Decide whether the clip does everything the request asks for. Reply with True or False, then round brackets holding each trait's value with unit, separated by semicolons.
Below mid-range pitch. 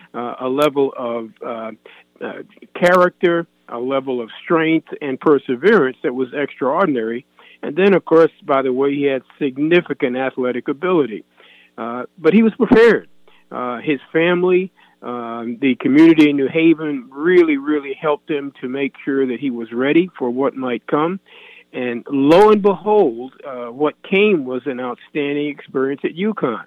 False (145 Hz)